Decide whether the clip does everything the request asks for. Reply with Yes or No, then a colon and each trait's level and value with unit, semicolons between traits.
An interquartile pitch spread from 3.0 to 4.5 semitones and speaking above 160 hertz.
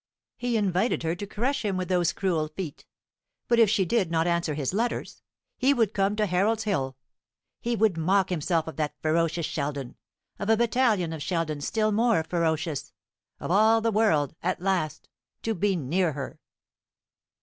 No: average, 5.1 semitones; medium, 185 Hz